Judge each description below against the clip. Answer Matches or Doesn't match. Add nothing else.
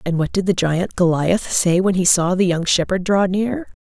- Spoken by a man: Doesn't match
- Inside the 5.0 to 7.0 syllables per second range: Doesn't match